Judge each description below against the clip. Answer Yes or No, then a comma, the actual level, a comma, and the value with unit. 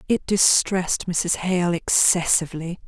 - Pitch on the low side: No, medium, 185 Hz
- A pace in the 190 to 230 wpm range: No, slow, 105 wpm